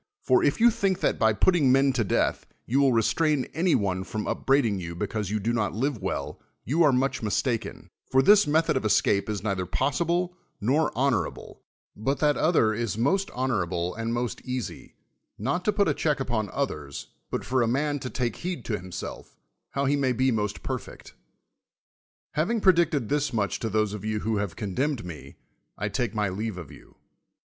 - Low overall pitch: Yes, low, 120 Hz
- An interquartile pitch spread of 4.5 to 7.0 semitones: Yes, wide, 5.5 semitones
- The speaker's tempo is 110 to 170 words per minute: No, average, 190 wpm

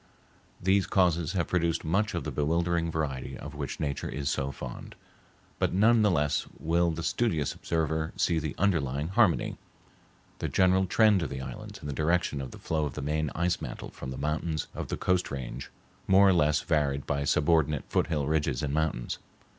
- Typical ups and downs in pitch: Yes, average, 3.4 semitones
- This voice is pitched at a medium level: No, very low, 80 Hz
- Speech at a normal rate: Yes, average, 185 wpm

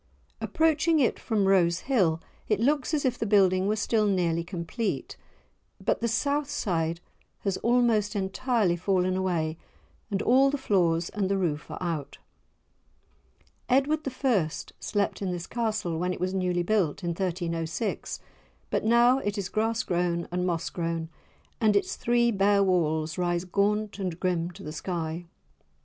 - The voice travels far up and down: No, average, 4.5 semitones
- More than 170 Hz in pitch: Yes, high, 190 Hz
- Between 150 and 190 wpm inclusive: Yes, average, 155 wpm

